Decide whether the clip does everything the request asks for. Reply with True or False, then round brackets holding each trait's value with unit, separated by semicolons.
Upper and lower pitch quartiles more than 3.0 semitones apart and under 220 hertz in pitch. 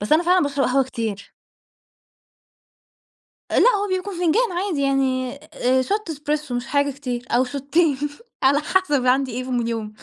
False (4.5 semitones; 275 Hz)